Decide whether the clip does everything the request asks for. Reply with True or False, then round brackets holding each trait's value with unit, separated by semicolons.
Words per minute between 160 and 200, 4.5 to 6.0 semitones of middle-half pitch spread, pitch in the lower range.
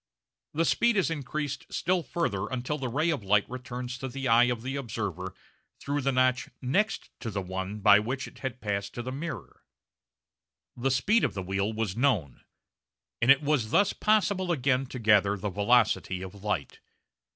True (180 wpm; 5.4 semitones; 125 Hz)